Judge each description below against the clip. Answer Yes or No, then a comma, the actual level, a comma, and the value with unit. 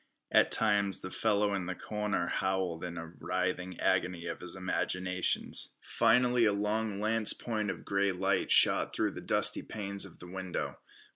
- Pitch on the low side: Yes, very low, 95 Hz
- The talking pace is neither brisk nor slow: Yes, average, 165 wpm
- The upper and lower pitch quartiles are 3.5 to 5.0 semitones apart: No, narrow, 2.5 semitones